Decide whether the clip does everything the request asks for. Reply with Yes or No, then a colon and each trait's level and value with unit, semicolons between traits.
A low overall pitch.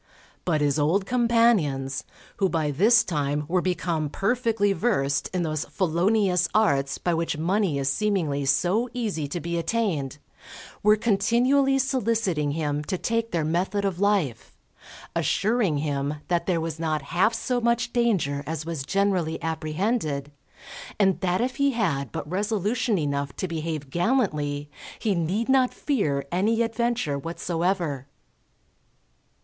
No: medium, 180 Hz